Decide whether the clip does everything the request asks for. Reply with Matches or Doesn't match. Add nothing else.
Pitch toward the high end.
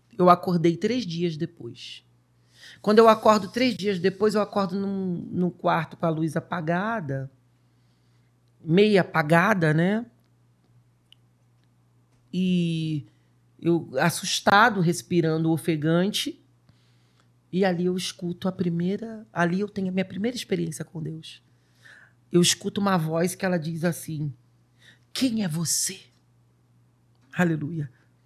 Doesn't match